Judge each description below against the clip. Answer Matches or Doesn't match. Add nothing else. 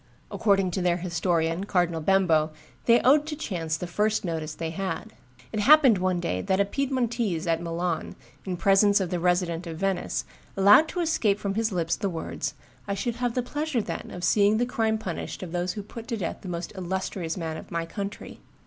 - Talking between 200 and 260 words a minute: Matches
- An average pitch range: Matches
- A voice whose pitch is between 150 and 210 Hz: Matches